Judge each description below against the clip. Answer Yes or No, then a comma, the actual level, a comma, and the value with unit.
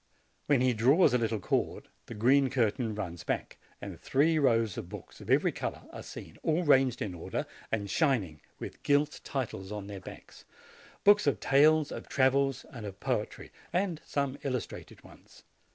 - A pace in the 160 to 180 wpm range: Yes, average, 170 wpm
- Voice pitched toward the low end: Yes, low, 130 Hz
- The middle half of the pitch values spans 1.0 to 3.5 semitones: No, average, 5.3 semitones